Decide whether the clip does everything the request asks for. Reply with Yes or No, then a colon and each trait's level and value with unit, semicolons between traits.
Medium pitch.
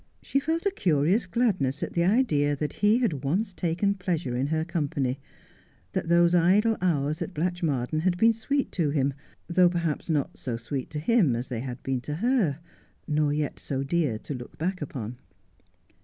Yes: medium, 160 Hz